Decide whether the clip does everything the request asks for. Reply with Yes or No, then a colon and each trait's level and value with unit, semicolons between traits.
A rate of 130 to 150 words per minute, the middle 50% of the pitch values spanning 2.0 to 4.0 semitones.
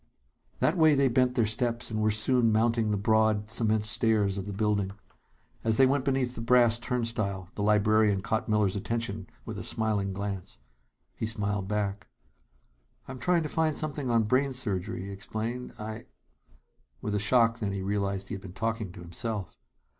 No: average, 180 wpm; average, 2.8 semitones